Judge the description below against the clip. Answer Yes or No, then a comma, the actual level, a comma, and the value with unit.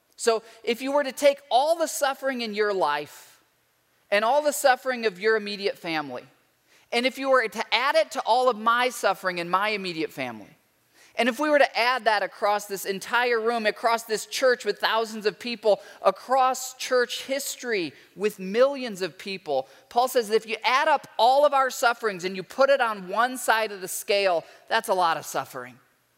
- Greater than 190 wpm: Yes, average, 200 wpm